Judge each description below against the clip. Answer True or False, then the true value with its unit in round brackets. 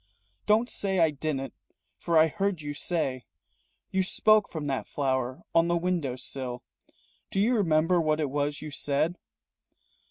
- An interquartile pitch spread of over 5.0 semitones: False (4.5 semitones)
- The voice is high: False (155 Hz)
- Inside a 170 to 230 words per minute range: False (155 wpm)